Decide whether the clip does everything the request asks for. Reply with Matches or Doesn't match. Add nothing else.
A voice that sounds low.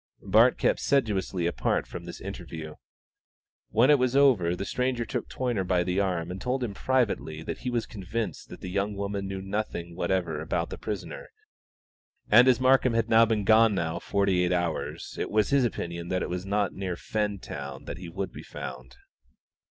Matches